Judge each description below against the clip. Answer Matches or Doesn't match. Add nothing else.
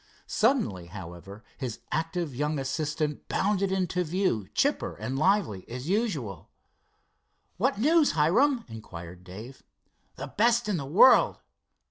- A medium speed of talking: Doesn't match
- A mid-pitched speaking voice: Matches